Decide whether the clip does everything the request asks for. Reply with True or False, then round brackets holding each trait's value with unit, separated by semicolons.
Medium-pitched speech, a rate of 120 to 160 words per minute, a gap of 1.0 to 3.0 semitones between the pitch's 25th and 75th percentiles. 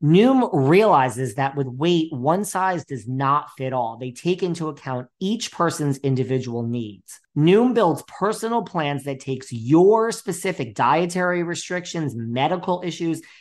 False (160 Hz; 140 wpm; 5.6 semitones)